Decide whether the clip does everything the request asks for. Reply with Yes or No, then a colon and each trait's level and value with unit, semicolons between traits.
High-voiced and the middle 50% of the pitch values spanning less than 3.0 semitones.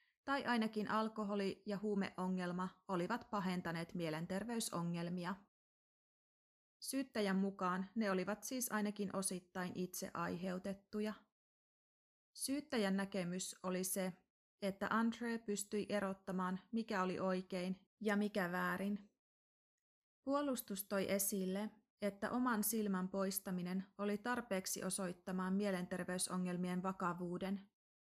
Yes: high, 195 Hz; narrow, 2.4 semitones